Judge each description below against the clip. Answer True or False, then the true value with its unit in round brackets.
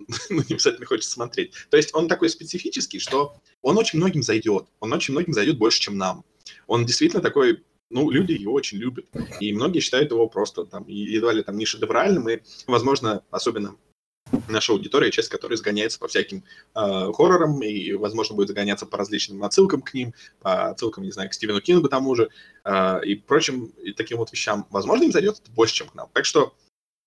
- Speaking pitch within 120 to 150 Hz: True (140 Hz)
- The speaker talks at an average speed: False (195 wpm)